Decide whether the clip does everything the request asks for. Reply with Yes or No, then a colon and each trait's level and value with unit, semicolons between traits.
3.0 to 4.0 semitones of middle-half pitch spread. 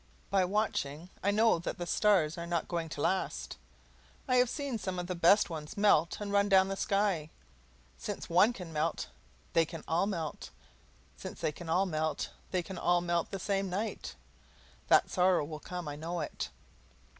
Yes: average, 3.3 semitones